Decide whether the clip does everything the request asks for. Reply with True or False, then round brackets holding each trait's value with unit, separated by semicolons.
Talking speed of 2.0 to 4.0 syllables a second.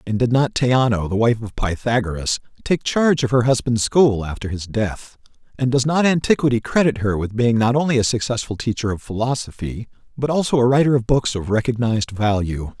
False (5.5 syllables/s)